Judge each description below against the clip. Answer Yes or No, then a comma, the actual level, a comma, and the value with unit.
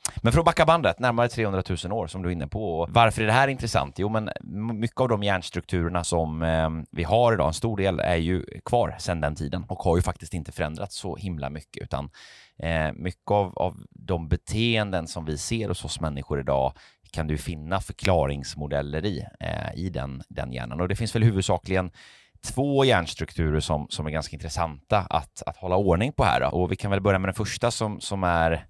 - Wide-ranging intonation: No, average, 5.0 semitones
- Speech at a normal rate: No, fast, 215 wpm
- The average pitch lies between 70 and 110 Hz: Yes, very low, 90 Hz